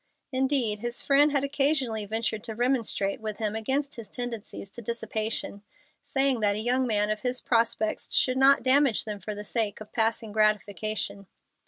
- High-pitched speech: Yes, high, 225 Hz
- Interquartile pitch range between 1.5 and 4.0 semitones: Yes, average, 3.5 semitones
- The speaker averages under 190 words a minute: Yes, average, 170 wpm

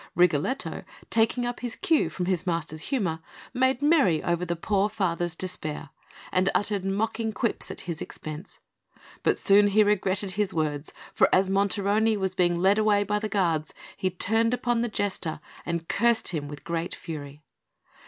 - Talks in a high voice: Yes, high, 195 Hz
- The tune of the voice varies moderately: Yes, average, 4.2 semitones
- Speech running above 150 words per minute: Yes, average, 165 wpm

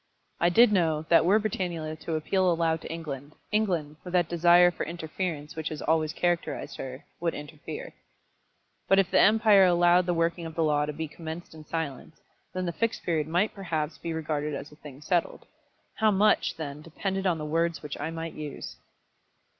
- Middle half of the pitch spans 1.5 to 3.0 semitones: Yes, narrow, 2.6 semitones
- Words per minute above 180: Yes, average, 190 wpm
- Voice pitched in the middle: Yes, medium, 165 Hz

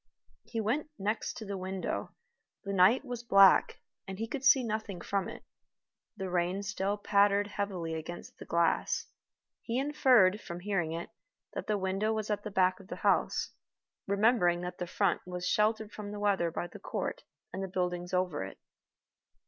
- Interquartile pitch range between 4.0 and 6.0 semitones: No, average, 2.9 semitones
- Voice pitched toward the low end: No, high, 195 Hz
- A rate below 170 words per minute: No, average, 175 wpm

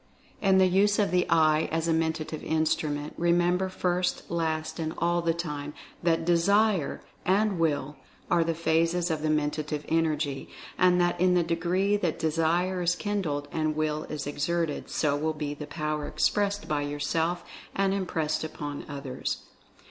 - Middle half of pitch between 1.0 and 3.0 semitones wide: Yes, average, 2.7 semitones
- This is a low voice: No, medium, 165 Hz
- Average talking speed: Yes, average, 165 wpm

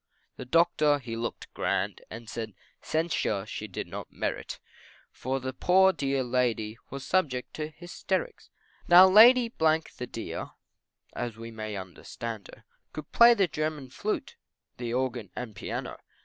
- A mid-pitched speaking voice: No, low, 130 Hz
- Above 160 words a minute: No, average, 145 wpm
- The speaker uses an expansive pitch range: Yes, wide, 6.7 semitones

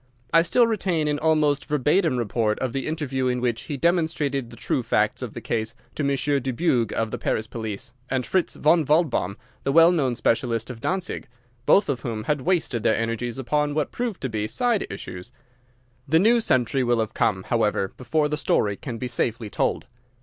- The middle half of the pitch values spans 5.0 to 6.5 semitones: Yes, wide, 5.5 semitones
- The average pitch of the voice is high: No, low, 135 Hz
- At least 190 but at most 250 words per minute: Yes, average, 195 wpm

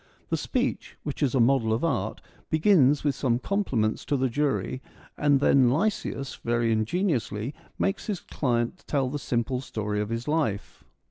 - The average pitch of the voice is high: No, low, 130 Hz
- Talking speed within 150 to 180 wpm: Yes, average, 160 wpm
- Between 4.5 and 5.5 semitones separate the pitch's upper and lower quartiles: No, average, 4.1 semitones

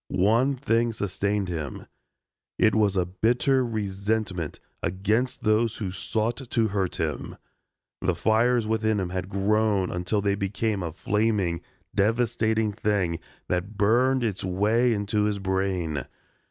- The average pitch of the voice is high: No, low, 105 Hz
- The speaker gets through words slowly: Yes, slow, 130 wpm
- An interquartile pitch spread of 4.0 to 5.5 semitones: No, average, 2.9 semitones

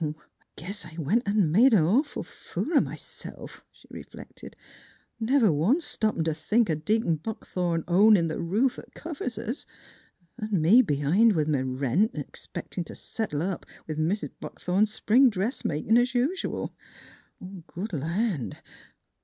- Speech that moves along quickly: No, average, 145 wpm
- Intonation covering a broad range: Yes, wide, 6.2 semitones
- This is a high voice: Yes, high, 200 Hz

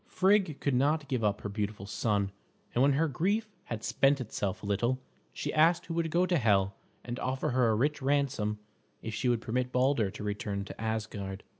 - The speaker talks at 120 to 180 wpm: No, average, 200 wpm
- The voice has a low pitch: Yes, low, 125 Hz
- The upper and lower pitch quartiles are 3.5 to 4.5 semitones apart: No, wide, 5.5 semitones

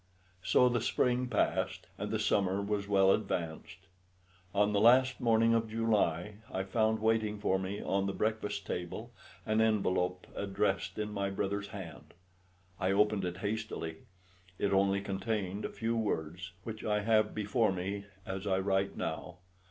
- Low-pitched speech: Yes, low, 100 Hz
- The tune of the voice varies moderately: No, narrow, 2.3 semitones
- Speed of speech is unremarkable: Yes, average, 155 wpm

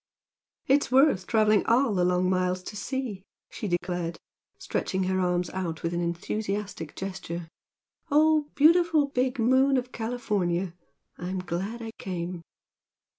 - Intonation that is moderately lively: No, wide, 6.0 semitones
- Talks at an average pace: No, slow, 130 wpm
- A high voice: Yes, high, 195 Hz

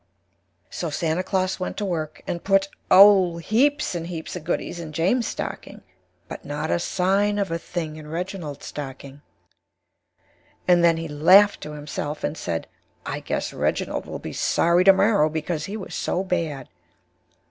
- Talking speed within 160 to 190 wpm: Yes, average, 165 wpm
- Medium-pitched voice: Yes, medium, 170 Hz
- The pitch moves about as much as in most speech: Yes, average, 3.8 semitones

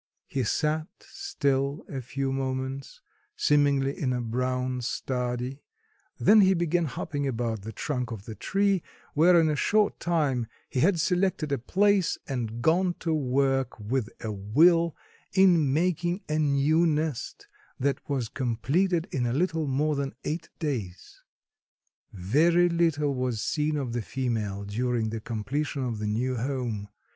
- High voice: No, medium, 140 Hz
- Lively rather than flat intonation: No, average, 4.8 semitones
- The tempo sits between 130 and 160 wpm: Yes, average, 150 wpm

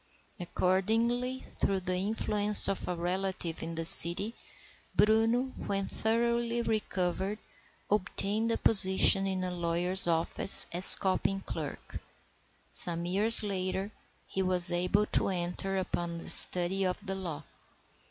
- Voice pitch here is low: No, high, 190 Hz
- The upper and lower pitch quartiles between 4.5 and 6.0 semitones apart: No, average, 2.9 semitones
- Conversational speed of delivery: No, slow, 125 wpm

